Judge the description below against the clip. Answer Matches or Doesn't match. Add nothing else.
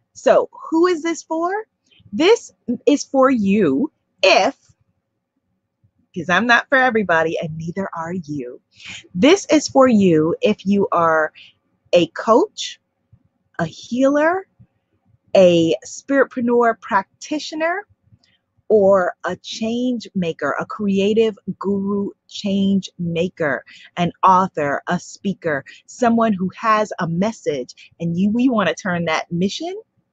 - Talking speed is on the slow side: Matches